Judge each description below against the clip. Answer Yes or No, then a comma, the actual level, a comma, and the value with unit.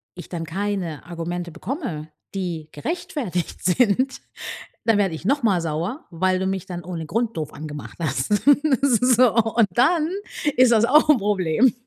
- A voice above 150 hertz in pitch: Yes, high, 190 Hz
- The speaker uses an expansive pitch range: Yes, wide, 6.1 semitones